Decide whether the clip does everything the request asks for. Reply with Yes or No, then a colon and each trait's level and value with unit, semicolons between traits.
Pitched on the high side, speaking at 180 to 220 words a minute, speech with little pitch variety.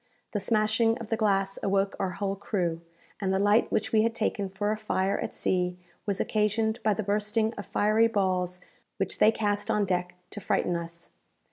Yes: high, 205 Hz; average, 195 wpm; narrow, 2.3 semitones